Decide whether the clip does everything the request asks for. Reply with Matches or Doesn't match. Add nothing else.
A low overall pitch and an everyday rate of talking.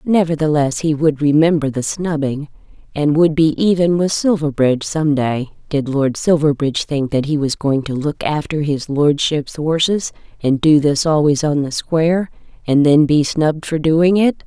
Doesn't match